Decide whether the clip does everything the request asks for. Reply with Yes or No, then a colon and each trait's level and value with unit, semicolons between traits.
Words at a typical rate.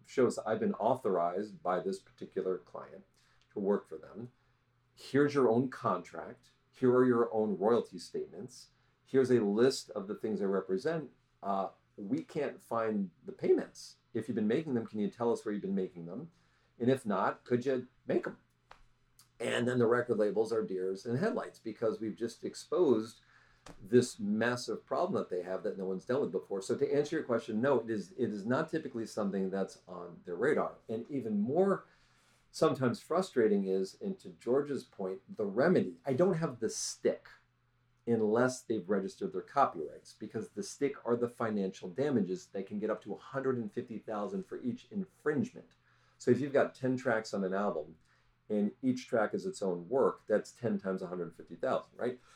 Yes: average, 190 wpm